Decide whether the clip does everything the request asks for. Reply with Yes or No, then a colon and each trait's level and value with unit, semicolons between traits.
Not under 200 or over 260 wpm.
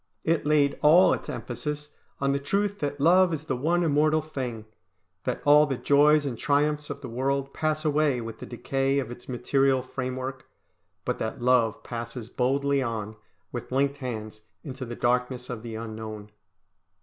No: average, 170 wpm